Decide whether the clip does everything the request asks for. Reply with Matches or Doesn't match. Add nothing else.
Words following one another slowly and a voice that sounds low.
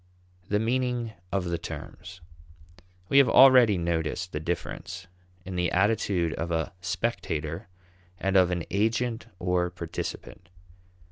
Matches